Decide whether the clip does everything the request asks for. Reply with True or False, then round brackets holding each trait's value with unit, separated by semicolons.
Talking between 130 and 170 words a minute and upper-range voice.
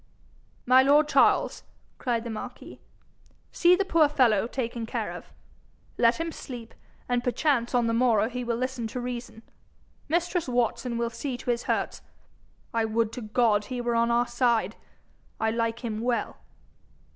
True (160 wpm; 240 Hz)